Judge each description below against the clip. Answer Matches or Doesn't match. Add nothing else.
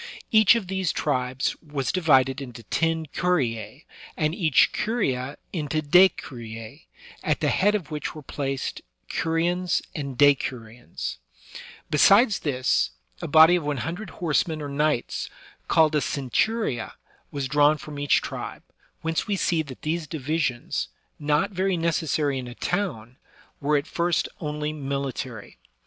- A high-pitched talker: Doesn't match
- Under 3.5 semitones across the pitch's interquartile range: Doesn't match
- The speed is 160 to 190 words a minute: Doesn't match